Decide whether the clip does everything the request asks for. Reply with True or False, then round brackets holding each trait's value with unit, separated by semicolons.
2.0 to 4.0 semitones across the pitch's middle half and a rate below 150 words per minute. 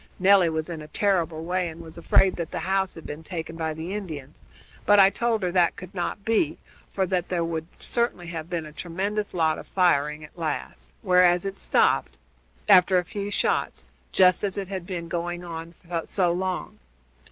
False (2.7 semitones; 195 wpm)